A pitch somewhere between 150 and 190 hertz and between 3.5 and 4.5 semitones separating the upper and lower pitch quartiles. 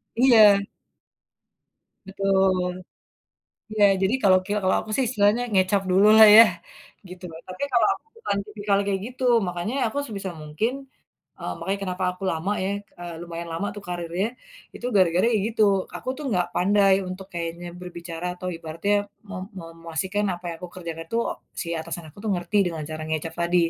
No: medium, 185 Hz; average, 3.1 semitones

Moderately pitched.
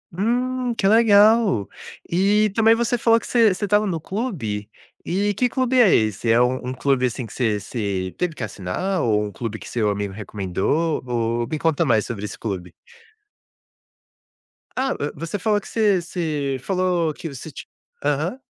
Yes: medium, 160 Hz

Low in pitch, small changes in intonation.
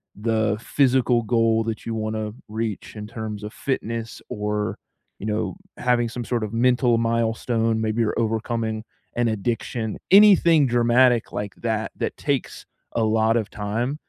Yes: low, 115 Hz; narrow, 1.7 semitones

